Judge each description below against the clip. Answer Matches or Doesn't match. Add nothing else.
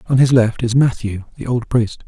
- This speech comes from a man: Matches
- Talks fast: Matches